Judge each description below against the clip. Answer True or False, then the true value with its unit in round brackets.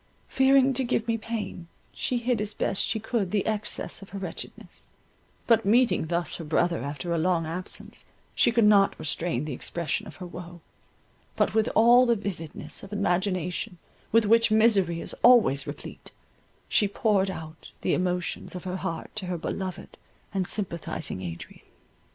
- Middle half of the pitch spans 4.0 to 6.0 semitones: True (4.3 semitones)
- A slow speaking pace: False (165 wpm)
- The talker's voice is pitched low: False (190 Hz)